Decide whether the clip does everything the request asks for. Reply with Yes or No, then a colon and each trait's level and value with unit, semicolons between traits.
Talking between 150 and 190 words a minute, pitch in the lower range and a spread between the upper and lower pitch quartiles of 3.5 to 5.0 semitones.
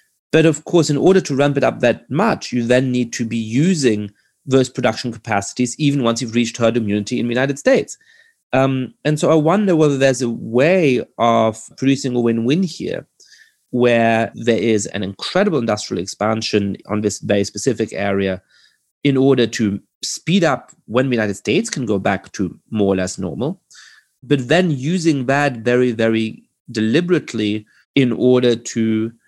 Yes: average, 170 wpm; low, 120 Hz; average, 4.2 semitones